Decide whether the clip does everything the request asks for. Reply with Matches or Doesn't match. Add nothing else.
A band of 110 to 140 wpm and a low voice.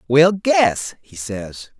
Matches